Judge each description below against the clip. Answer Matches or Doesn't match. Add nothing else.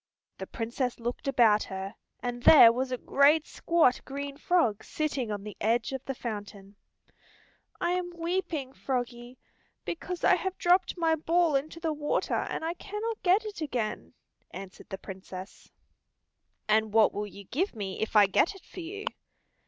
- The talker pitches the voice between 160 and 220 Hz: Doesn't match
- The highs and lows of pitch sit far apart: Matches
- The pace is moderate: Matches